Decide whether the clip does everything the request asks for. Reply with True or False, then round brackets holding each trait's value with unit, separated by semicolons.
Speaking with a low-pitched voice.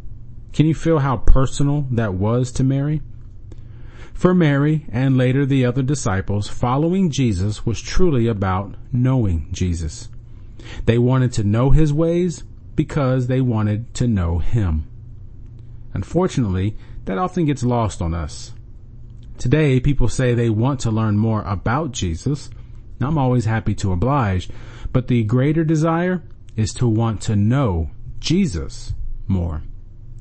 True (115 Hz)